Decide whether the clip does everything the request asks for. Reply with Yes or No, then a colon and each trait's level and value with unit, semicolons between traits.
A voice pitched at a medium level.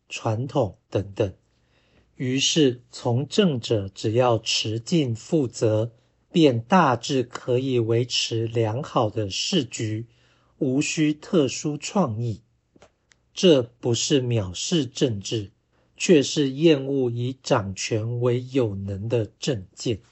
No: low, 120 Hz